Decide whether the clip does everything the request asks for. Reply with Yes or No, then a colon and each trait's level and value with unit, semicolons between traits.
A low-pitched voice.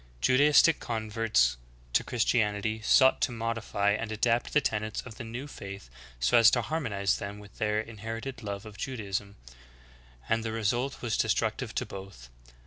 Yes: low, 110 Hz